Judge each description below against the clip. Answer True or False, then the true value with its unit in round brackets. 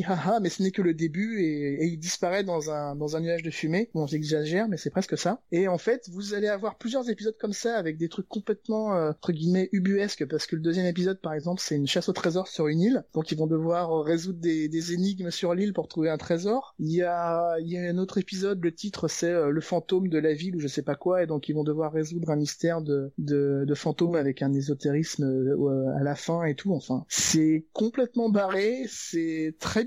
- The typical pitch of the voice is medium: True (170 Hz)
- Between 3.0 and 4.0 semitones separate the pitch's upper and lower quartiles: True (3.7 semitones)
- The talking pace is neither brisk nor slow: False (240 wpm)